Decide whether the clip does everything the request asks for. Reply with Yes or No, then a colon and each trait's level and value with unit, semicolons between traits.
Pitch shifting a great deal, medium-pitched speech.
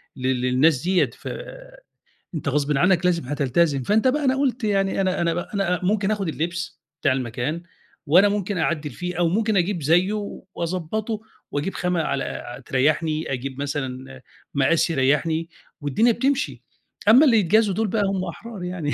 Yes: wide, 5.8 semitones; medium, 170 Hz